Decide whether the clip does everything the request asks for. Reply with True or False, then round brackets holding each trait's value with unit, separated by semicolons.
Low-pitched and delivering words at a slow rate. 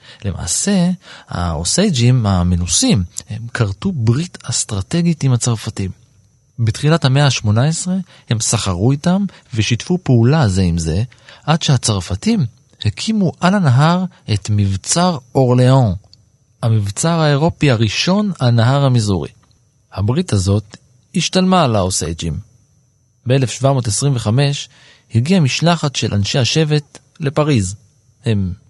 True (125 Hz; 95 wpm)